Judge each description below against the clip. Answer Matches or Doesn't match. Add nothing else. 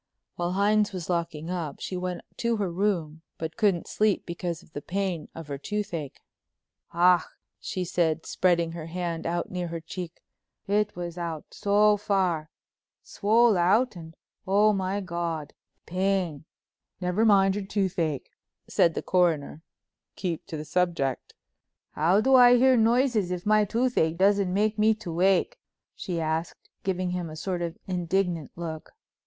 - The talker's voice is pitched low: Doesn't match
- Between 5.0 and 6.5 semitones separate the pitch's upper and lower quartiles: Doesn't match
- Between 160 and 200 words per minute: Doesn't match